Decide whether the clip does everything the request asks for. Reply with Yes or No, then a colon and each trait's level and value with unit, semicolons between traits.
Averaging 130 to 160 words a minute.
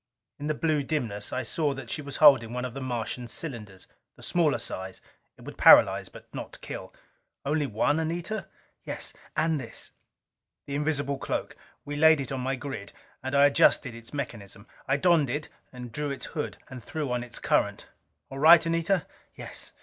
No: average, 185 wpm